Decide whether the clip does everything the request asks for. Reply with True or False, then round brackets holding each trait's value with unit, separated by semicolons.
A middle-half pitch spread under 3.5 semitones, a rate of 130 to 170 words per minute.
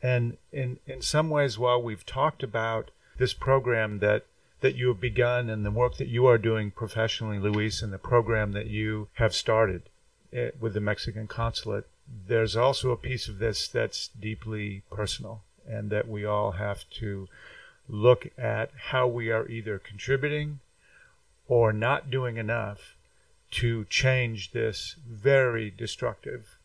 True (2.8 semitones; 150 wpm)